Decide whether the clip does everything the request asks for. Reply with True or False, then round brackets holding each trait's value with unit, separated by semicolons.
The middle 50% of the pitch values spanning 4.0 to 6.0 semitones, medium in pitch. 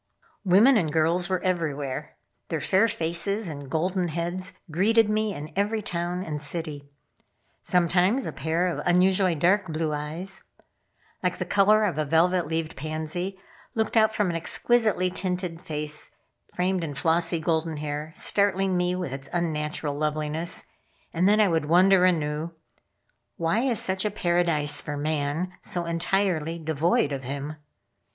False (3.4 semitones; 170 Hz)